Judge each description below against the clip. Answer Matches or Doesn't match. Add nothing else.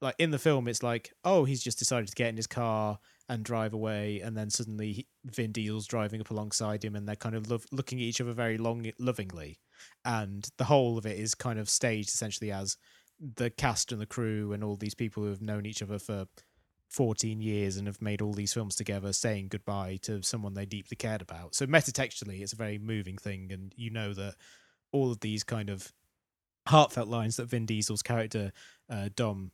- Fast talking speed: Matches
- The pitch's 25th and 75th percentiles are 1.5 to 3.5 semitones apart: Matches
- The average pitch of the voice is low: Matches